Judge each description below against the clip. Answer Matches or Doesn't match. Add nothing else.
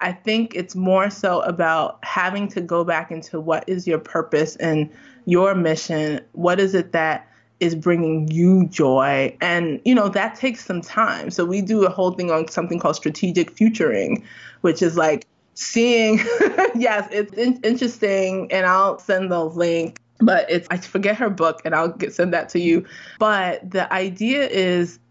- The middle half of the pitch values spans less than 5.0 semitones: Matches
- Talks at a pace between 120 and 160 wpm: Doesn't match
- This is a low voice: Doesn't match